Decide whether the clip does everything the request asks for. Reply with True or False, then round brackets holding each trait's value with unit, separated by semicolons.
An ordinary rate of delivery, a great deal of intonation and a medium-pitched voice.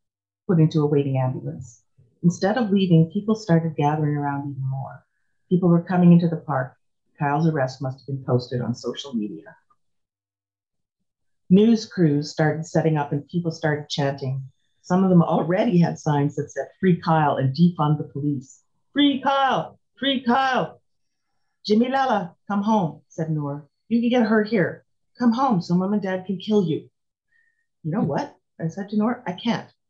True (170 wpm; 6.2 semitones; 160 Hz)